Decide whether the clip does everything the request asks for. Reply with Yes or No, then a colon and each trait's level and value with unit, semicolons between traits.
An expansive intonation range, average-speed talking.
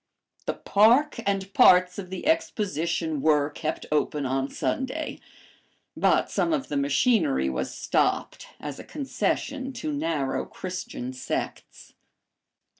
No: wide, 8.2 semitones; slow, 120 wpm